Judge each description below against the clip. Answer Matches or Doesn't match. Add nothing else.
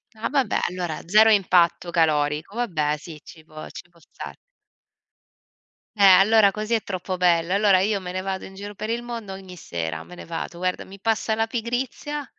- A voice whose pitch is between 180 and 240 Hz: Matches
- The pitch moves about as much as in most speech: Matches